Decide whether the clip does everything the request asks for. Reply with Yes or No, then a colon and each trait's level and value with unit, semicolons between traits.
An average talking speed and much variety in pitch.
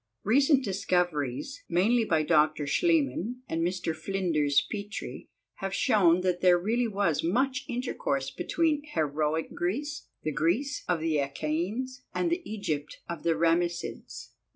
No: slow, 130 wpm; wide, 7.4 semitones